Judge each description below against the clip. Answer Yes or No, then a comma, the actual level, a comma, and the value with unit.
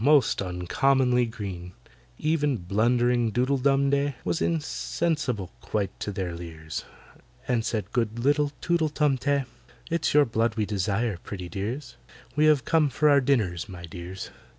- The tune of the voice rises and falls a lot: Yes, wide, 6.3 semitones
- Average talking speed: Yes, average, 150 wpm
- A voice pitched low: Yes, low, 120 Hz